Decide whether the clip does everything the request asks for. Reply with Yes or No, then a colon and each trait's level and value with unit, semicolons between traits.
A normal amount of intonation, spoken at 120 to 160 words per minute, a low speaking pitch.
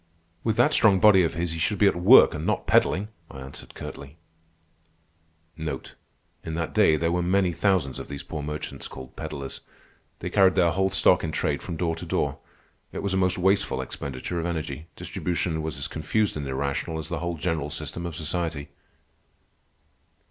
No: average, 3.1 semitones; average, 185 wpm; very low, 85 Hz